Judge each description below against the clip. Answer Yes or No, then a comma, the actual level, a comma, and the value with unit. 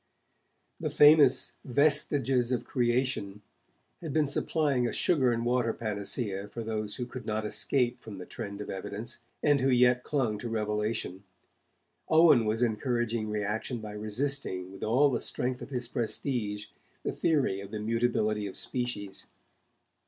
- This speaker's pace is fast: No, average, 150 wpm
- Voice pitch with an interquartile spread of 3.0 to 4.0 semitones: Yes, average, 3.5 semitones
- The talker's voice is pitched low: Yes, low, 120 Hz